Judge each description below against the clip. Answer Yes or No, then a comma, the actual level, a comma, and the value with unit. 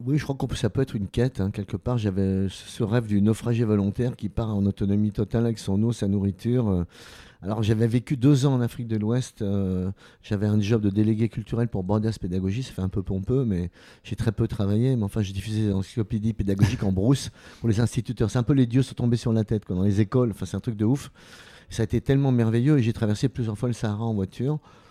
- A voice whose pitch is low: Yes, low, 110 Hz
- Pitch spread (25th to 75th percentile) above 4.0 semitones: No, average, 3.2 semitones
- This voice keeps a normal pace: No, fast, 250 wpm